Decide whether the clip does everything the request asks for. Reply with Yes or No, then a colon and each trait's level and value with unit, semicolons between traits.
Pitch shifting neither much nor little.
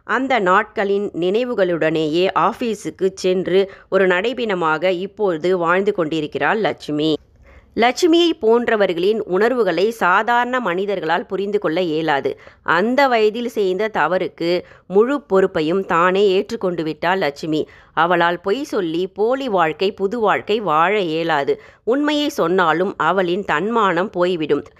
Yes: average, 4.8 semitones